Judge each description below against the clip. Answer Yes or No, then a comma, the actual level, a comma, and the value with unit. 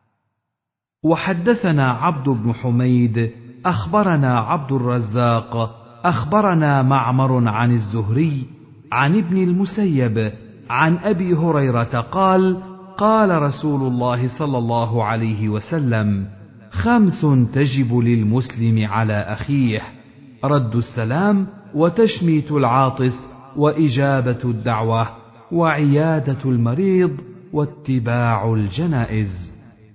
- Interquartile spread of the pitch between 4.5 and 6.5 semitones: Yes, wide, 5.5 semitones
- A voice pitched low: Yes, low, 130 Hz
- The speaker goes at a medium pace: Yes, average, 80 wpm